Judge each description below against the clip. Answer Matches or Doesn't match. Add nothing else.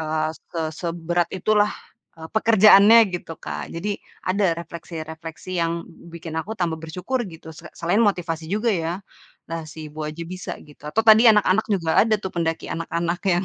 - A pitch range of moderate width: Matches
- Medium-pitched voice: Matches